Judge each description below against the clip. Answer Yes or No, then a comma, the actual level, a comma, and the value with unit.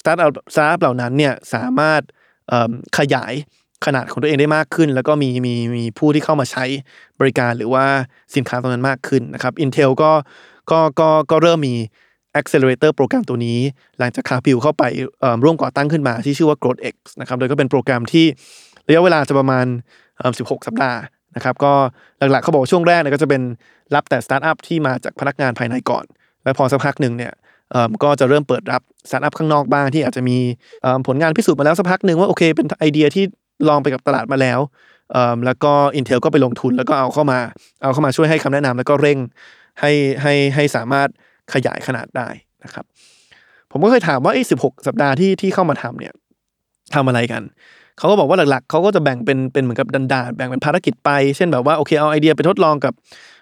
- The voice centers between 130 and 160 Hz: Yes, medium, 140 Hz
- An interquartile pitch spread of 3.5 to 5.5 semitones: No, average, 3.0 semitones